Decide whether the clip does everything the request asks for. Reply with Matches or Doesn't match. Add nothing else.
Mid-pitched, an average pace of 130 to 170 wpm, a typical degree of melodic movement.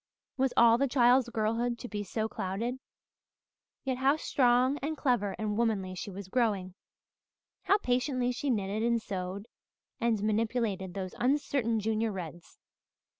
Doesn't match